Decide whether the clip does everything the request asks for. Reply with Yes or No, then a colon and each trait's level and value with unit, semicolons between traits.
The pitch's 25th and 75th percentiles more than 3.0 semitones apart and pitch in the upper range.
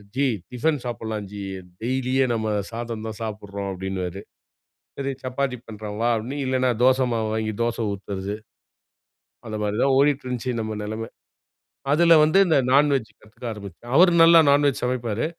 No: average, 3.8 semitones; low, 115 Hz